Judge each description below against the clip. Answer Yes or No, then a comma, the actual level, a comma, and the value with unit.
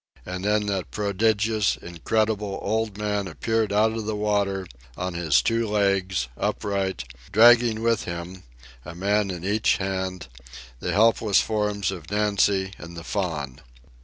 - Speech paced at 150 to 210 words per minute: No, average, 140 wpm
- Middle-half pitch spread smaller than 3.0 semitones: Yes, narrow, 2.6 semitones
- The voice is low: Yes, low, 100 Hz